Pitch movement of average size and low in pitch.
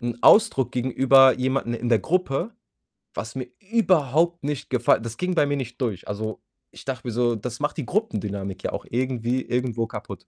Yes: average, 3.5 semitones; low, 125 Hz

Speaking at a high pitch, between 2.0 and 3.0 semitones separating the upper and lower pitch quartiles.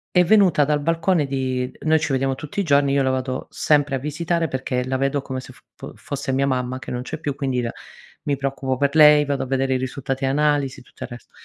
No: medium, 140 Hz; narrow, 2.3 semitones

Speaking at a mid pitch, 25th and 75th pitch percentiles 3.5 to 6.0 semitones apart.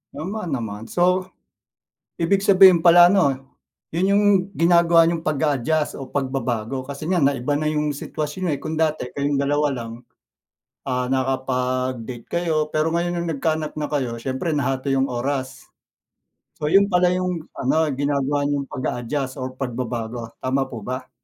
Yes: medium, 145 Hz; average, 4.2 semitones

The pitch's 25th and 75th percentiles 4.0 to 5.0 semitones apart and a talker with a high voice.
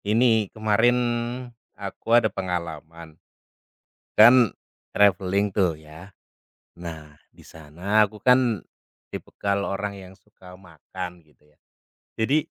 No: average, 4.3 semitones; very low, 95 Hz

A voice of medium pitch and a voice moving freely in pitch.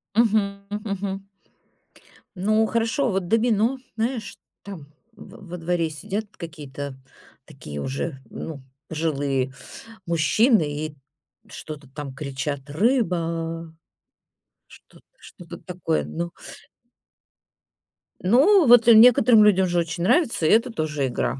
Yes: medium, 180 Hz; wide, 6.1 semitones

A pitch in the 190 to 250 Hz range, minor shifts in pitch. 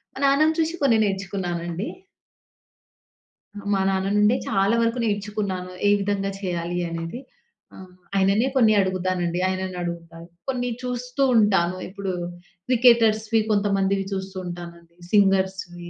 No: high, 195 Hz; average, 3.3 semitones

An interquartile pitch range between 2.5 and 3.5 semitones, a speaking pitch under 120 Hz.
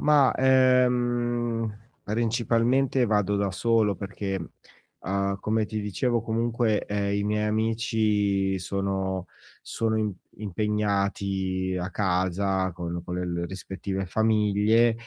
Yes: average, 2.9 semitones; low, 105 Hz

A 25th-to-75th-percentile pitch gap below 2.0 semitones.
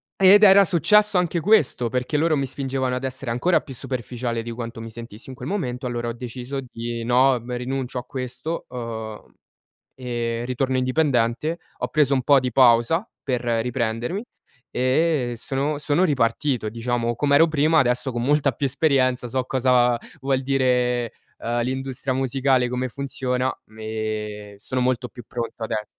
No: narrow, 2.6 semitones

